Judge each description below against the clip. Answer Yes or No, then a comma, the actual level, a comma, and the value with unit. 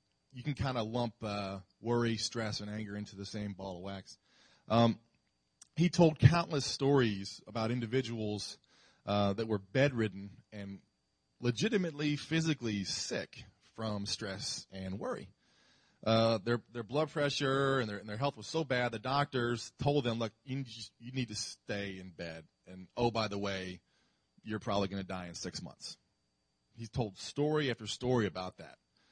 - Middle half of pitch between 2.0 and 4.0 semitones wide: No, average, 4.5 semitones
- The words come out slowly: No, average, 165 wpm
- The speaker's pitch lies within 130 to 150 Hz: No, low, 115 Hz